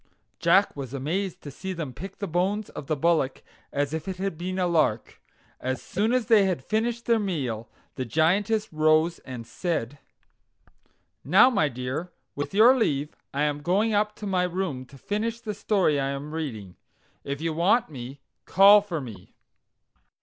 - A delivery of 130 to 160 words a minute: No, average, 175 wpm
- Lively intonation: Yes, wide, 6.3 semitones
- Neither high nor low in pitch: Yes, medium, 165 Hz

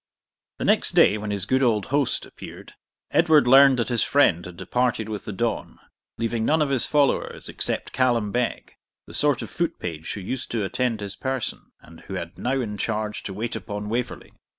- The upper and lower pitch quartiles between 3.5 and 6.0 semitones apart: Yes, average, 4.1 semitones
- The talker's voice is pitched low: Yes, low, 115 Hz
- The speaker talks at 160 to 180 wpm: No, average, 195 wpm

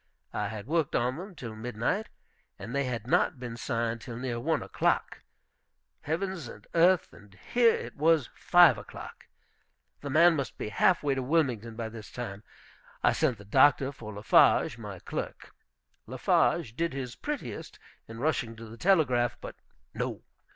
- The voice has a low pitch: Yes, low, 125 Hz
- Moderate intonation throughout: No, wide, 5.8 semitones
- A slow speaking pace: No, average, 165 wpm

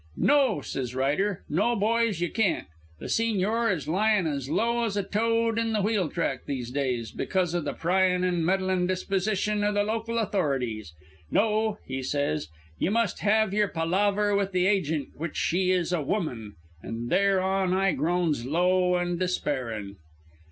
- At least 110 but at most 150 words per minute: No, average, 160 wpm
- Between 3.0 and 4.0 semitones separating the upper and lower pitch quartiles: No, average, 5.2 semitones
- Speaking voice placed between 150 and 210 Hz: Yes, medium, 185 Hz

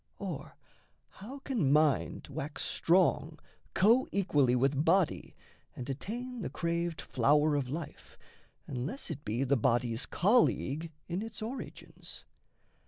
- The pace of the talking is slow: Yes, slow, 115 wpm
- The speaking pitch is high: No, medium, 155 Hz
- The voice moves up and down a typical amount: No, wide, 6.4 semitones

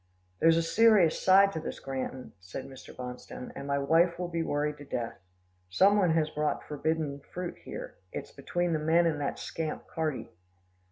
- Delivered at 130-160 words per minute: No, average, 180 wpm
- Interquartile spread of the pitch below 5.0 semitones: Yes, average, 3.4 semitones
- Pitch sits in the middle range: Yes, medium, 155 Hz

